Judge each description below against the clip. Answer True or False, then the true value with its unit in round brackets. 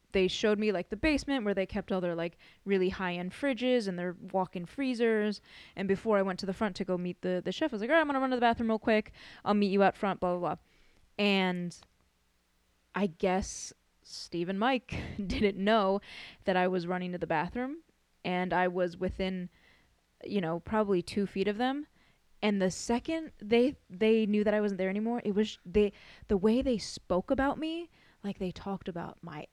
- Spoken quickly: True (215 wpm)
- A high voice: True (195 Hz)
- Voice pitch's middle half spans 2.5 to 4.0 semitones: True (3.4 semitones)